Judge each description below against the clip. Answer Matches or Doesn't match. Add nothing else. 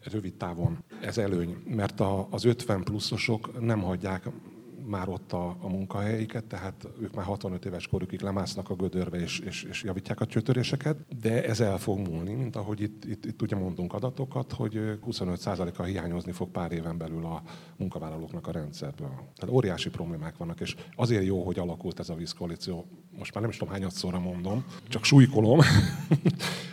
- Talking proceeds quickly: Matches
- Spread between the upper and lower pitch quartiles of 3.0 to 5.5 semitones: Matches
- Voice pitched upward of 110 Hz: Doesn't match